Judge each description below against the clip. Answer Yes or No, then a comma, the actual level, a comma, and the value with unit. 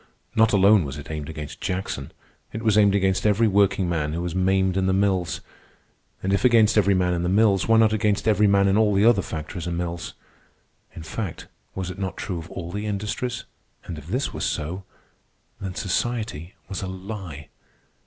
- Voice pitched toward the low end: Yes, very low, 95 Hz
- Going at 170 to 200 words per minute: Yes, average, 195 wpm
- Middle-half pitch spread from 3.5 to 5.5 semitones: No, average, 3.1 semitones